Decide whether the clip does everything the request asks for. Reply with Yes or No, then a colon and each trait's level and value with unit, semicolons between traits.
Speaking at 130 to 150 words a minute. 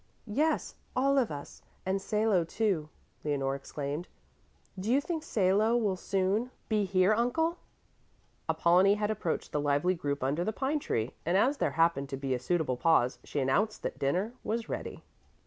No: average, 165 wpm